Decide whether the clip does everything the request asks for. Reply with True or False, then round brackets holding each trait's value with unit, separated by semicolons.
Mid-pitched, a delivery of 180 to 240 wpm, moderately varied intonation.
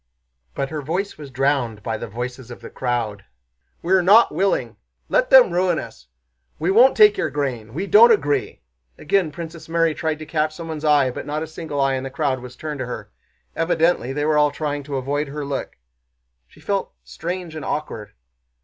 True (150 Hz; 195 wpm; 4.1 semitones)